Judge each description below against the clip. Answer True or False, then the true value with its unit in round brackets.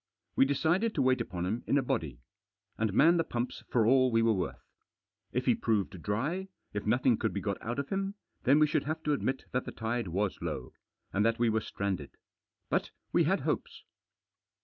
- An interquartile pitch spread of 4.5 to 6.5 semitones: True (5.4 semitones)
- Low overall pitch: True (120 Hz)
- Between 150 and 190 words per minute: False (205 wpm)